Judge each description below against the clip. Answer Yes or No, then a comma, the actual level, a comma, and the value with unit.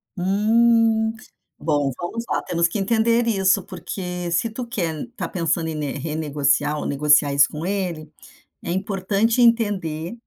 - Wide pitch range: Yes, wide, 6.1 semitones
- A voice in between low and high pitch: Yes, medium, 180 Hz